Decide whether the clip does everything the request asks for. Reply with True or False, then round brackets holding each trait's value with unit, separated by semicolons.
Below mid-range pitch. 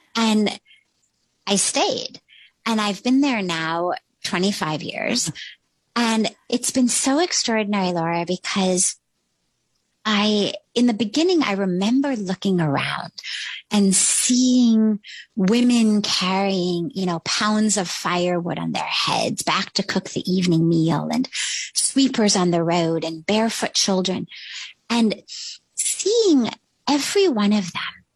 False (205 Hz)